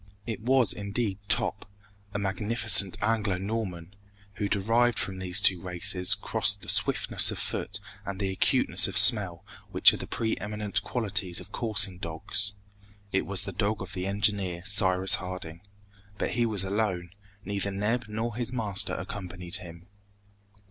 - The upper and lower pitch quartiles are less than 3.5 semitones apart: Yes, narrow, 2.5 semitones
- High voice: No, low, 100 Hz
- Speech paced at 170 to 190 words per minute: No, average, 150 wpm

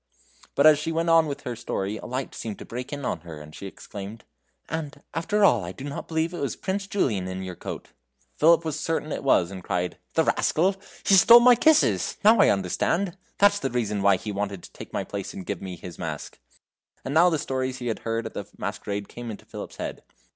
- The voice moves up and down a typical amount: No, wide, 8.8 semitones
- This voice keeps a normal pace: No, fast, 230 wpm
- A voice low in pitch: Yes, low, 130 Hz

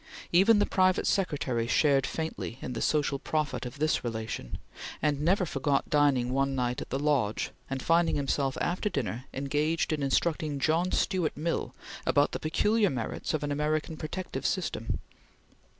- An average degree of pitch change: Yes, average, 3.5 semitones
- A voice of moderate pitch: Yes, medium, 150 Hz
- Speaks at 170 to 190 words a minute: No, average, 160 wpm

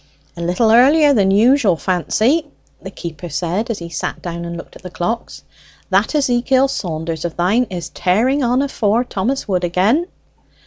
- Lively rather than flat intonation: Yes, wide, 6.3 semitones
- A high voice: Yes, high, 200 Hz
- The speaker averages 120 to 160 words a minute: No, average, 170 wpm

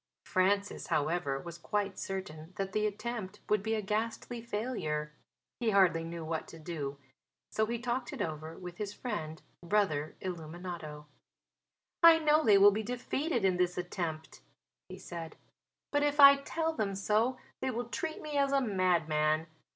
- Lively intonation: Yes, wide, 6.2 semitones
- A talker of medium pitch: No, high, 195 Hz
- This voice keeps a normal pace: Yes, average, 160 wpm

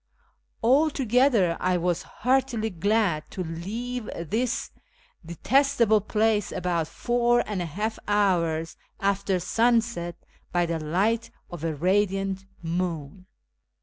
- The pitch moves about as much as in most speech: Yes, average, 5.0 semitones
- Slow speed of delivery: Yes, slow, 110 wpm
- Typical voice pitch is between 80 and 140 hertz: No, high, 195 Hz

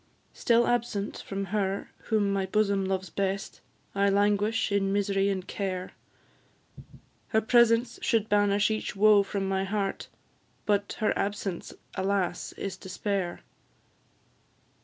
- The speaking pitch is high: Yes, high, 200 Hz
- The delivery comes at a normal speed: No, slow, 120 wpm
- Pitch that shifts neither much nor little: No, narrow, 1.5 semitones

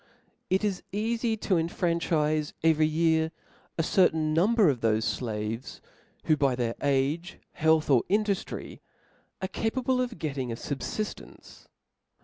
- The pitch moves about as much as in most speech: No, wide, 5.8 semitones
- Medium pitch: Yes, medium, 160 Hz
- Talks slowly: Yes, slow, 130 wpm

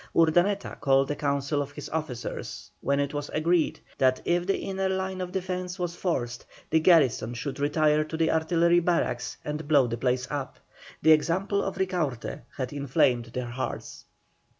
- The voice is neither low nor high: Yes, medium, 155 Hz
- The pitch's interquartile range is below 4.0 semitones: No, average, 4.6 semitones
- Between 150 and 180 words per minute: Yes, average, 170 wpm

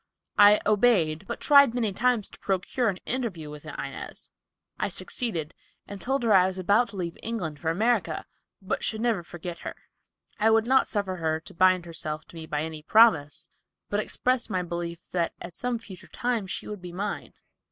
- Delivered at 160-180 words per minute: No, average, 190 wpm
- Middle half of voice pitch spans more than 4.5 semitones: Yes, average, 5.1 semitones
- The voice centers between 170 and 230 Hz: Yes, high, 190 Hz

